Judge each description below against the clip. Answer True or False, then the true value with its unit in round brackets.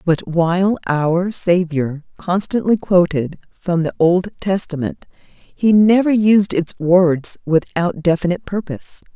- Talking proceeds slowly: True (120 wpm)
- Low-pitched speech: False (175 Hz)